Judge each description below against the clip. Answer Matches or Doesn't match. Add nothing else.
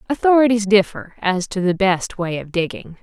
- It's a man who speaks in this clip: Doesn't match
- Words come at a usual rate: Matches